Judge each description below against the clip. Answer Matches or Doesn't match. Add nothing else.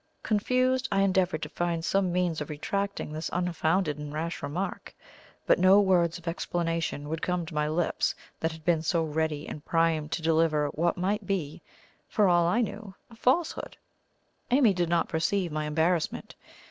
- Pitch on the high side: Doesn't match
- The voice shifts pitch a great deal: Doesn't match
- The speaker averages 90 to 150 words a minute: Doesn't match